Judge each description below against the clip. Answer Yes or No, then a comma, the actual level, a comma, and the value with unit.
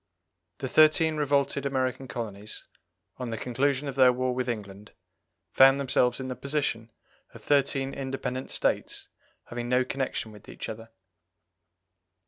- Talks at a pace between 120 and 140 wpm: Yes, slow, 135 wpm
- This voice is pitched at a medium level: No, low, 130 Hz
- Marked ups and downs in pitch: No, narrow, 2.5 semitones